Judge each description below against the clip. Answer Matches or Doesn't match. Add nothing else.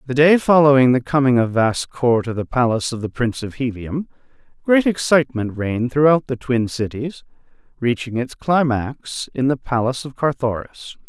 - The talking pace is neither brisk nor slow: Matches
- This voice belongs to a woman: Doesn't match